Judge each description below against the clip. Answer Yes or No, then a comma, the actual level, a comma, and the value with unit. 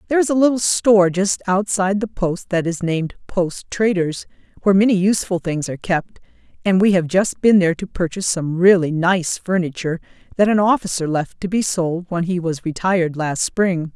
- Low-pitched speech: No, medium, 185 Hz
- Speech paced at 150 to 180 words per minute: No, average, 195 wpm